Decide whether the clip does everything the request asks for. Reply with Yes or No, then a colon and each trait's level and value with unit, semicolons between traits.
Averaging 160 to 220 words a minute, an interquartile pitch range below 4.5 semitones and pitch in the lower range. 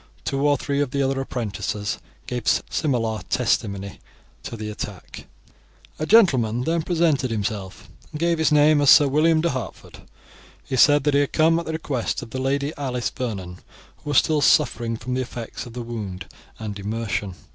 No: average, 185 wpm; average, 4.8 semitones; low, 130 Hz